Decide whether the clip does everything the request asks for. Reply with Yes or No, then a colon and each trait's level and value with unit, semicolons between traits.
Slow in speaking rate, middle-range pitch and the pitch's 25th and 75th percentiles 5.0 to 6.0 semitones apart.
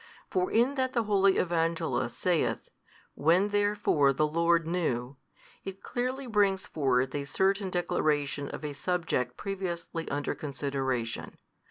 Yes: slow, 130 wpm; medium, 170 Hz; wide, 5.5 semitones